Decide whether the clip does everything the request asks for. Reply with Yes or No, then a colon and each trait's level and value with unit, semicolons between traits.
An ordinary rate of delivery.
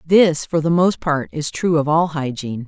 No: fast, 225 wpm